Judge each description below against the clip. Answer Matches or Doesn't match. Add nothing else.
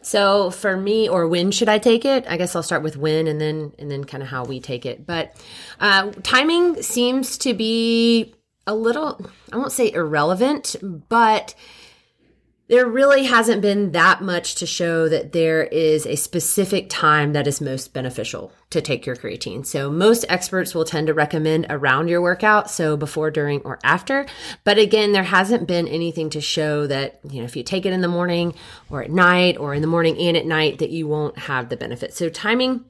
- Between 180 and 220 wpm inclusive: Matches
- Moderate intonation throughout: Doesn't match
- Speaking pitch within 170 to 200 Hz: Matches